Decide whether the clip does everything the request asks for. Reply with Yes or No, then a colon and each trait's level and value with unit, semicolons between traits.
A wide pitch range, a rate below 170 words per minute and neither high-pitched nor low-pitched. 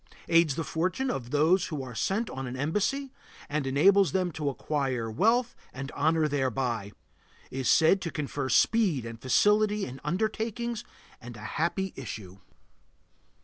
Yes: wide, 7.0 semitones; average, 145 wpm; medium, 150 Hz